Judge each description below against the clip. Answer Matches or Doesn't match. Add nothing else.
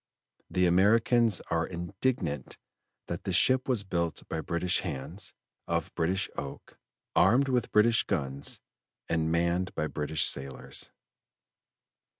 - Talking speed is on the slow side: Matches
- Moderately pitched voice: Doesn't match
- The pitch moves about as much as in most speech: Matches